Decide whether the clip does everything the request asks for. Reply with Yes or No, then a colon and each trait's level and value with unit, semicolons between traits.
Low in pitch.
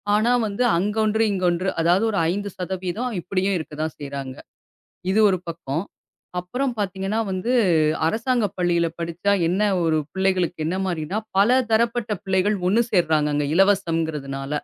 No: medium, 185 Hz